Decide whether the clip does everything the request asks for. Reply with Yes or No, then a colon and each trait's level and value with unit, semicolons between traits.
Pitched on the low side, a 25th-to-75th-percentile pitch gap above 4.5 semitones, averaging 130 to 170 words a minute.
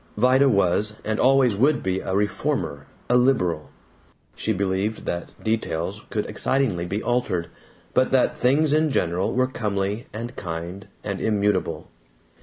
Yes: low, 105 Hz; average, 5.1 semitones; average, 140 wpm